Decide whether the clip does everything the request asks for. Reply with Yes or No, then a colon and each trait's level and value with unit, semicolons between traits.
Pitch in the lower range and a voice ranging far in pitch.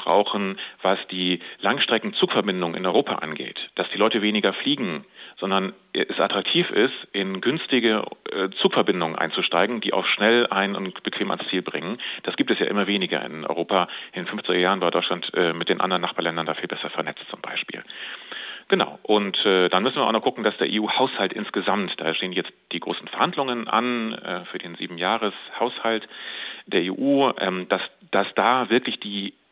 No: low, 100 Hz; average, 2.9 semitones